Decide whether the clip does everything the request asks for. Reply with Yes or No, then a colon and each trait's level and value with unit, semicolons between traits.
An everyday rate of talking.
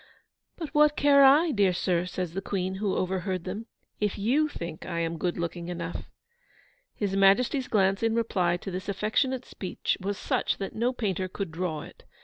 Yes: average, 180 wpm